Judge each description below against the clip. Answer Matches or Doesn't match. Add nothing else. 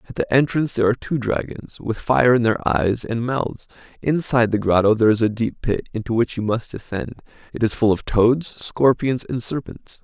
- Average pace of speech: Doesn't match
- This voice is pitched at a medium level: Doesn't match